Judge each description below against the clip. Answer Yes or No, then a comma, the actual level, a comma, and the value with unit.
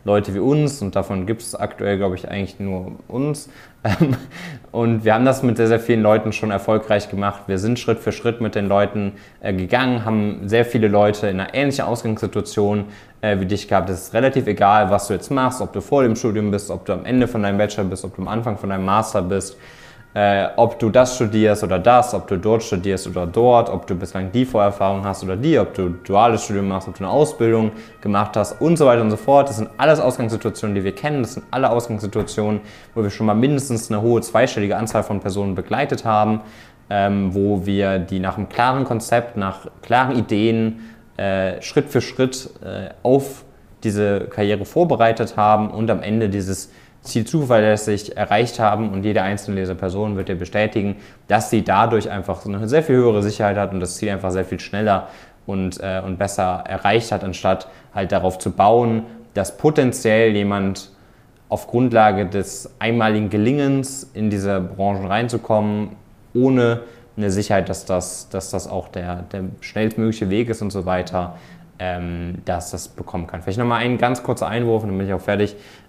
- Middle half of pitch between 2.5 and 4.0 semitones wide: Yes, average, 3.0 semitones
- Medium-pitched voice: No, low, 105 Hz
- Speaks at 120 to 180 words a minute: No, fast, 190 wpm